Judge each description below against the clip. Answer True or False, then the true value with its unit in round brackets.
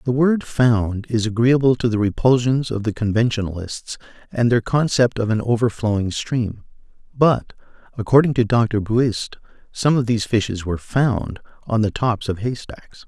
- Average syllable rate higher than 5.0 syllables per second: False (4.7 syllables/s)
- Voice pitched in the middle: False (115 Hz)